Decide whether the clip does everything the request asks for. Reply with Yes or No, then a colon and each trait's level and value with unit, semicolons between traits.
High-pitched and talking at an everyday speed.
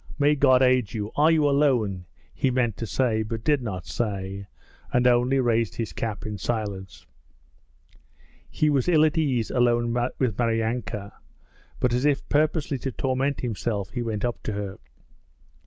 No: low, 120 Hz; average, 160 wpm